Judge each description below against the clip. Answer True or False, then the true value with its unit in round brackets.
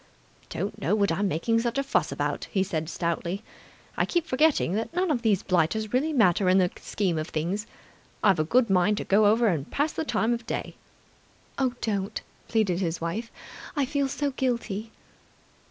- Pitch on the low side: False (210 Hz)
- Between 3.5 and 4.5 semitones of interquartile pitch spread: False (5.0 semitones)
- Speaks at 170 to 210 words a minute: True (185 wpm)